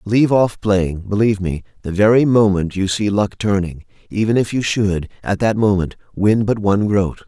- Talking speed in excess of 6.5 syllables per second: No, 5.1 syllables/s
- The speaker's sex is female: No, male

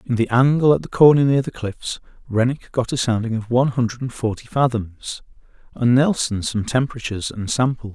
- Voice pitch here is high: No, low, 120 Hz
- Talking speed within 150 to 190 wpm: Yes, average, 180 wpm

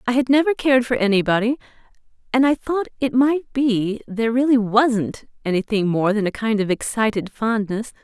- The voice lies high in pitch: Yes, high, 230 Hz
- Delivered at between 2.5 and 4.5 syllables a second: No, 5.2 syllables/s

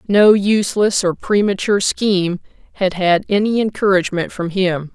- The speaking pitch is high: Yes, high, 195 Hz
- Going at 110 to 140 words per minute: Yes, slow, 135 wpm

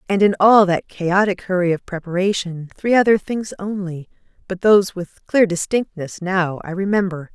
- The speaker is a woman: Yes, female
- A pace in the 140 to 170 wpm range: Yes, average, 165 wpm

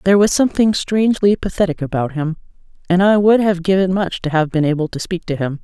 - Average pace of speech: No, fast, 225 wpm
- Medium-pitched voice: Yes, medium, 180 Hz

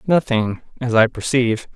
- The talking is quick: No, slow, 100 wpm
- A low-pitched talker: Yes, low, 120 Hz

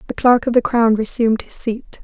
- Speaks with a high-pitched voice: Yes, high, 230 Hz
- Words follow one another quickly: Yes, fast, 235 wpm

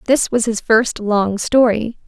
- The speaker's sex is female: Yes, female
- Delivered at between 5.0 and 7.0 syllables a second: No, 3.8 syllables/s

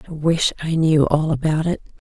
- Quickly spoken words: Yes, fast, 210 wpm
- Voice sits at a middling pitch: Yes, medium, 155 Hz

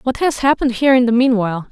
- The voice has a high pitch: Yes, high, 245 Hz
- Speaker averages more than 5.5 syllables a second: Yes, 7.6 syllables/s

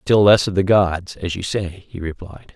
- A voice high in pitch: No, very low, 95 Hz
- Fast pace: Yes, fast, 235 wpm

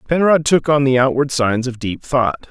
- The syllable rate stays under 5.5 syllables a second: Yes, 5.0 syllables/s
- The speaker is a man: Yes, male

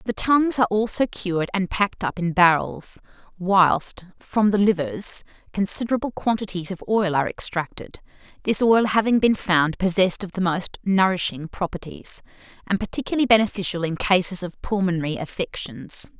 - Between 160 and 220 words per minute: No, average, 145 wpm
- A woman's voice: Yes, female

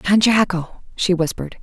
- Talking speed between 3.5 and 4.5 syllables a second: No, 4.8 syllables/s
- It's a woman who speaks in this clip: Yes, female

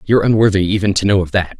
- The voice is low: Yes, low, 100 Hz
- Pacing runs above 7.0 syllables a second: Yes, 7.6 syllables/s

